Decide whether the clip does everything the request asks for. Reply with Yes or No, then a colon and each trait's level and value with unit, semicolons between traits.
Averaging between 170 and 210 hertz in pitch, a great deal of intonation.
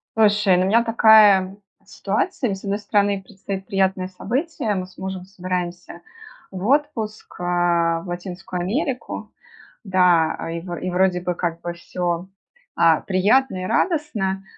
No: high, 190 Hz; average, 3.1 semitones